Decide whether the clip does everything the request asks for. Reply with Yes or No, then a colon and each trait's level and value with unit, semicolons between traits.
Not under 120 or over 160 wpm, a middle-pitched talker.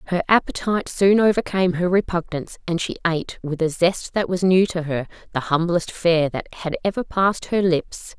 No: average, 190 wpm; medium, 175 Hz